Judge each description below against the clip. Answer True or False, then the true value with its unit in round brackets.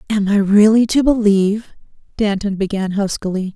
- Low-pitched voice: False (205 Hz)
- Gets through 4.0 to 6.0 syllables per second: True (5.1 syllables/s)